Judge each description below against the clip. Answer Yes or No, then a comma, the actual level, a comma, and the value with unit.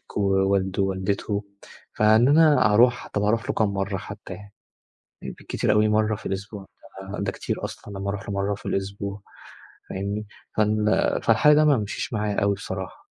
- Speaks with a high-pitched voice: No, low, 100 Hz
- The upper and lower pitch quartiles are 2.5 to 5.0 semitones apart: No, narrow, 1.6 semitones